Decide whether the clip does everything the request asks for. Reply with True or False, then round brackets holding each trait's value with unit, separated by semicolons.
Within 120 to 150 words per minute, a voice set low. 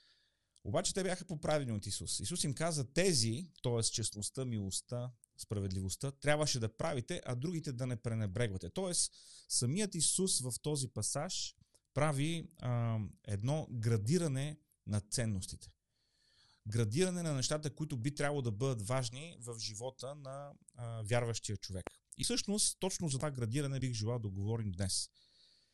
True (140 wpm; 125 Hz)